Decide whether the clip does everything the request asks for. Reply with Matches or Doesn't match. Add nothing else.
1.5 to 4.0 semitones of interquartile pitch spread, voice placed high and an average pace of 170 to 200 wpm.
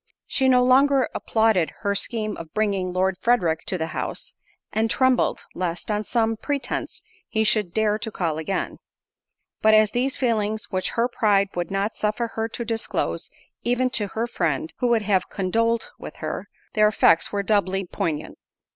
Matches